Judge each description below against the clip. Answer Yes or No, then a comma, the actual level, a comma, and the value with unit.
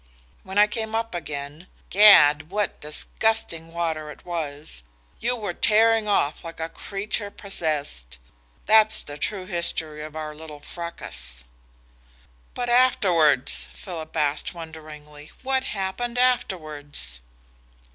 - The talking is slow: Yes, slow, 115 wpm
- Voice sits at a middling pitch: Yes, medium, 165 Hz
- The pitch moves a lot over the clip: Yes, wide, 5.7 semitones